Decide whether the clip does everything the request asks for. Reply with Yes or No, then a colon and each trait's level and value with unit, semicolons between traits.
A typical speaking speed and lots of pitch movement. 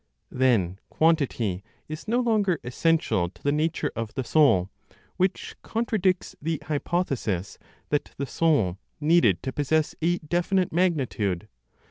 No: slow, 125 wpm; wide, 7.1 semitones